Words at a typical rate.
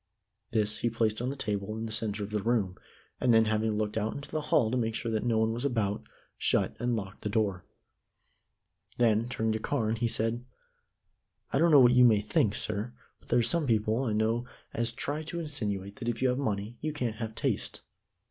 No: fast, 220 wpm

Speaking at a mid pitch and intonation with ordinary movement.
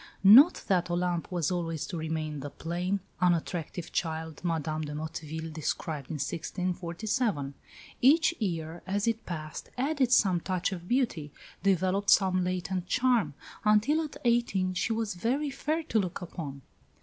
Yes: medium, 180 Hz; average, 5.0 semitones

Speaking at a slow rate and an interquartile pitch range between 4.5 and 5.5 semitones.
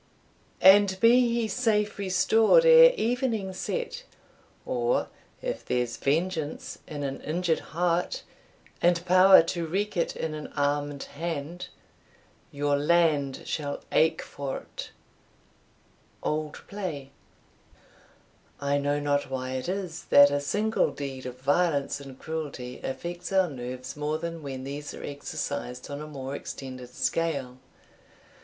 Yes: slow, 125 wpm; average, 4.9 semitones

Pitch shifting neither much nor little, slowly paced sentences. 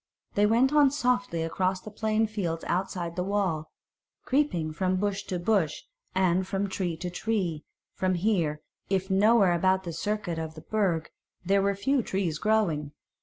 No: average, 3.8 semitones; average, 165 wpm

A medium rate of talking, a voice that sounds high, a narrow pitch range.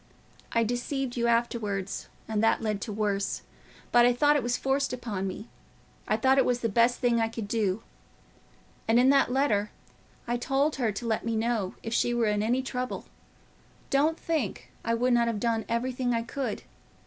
Yes: average, 190 wpm; high, 235 Hz; narrow, 2.3 semitones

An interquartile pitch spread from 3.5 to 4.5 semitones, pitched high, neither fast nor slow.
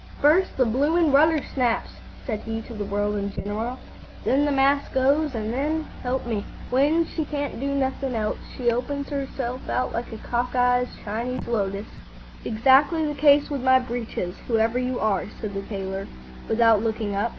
Yes: average, 4.1 semitones; very high, 250 Hz; average, 180 wpm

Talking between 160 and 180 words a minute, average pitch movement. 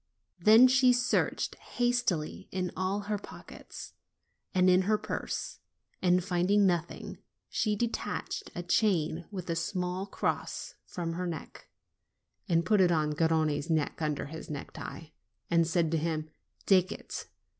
No: average, 145 wpm; average, 3.8 semitones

